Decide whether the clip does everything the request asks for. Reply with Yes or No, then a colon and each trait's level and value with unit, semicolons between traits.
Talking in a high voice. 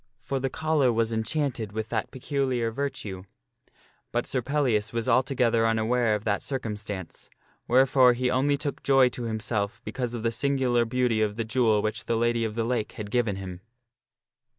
No: low, 120 Hz